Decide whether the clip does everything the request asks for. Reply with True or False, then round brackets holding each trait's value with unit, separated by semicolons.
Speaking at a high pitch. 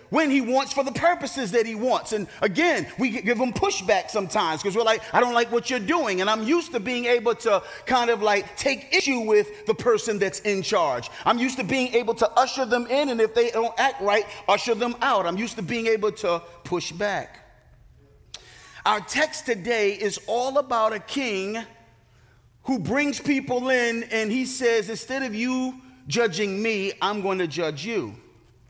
True (230 Hz)